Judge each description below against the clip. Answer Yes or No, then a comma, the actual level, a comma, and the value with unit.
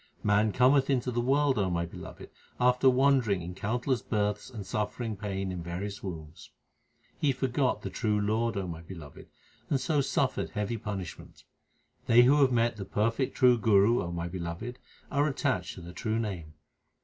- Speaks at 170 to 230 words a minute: Yes, average, 175 wpm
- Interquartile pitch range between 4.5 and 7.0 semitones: Yes, average, 4.9 semitones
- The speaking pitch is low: Yes, low, 110 Hz